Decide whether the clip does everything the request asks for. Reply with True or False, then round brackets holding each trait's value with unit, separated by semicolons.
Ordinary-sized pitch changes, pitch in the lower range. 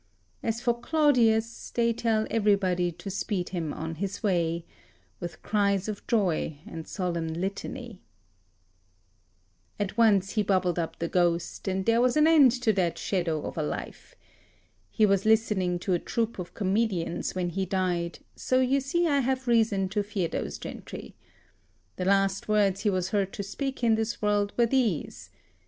False (4.0 semitones; 200 Hz)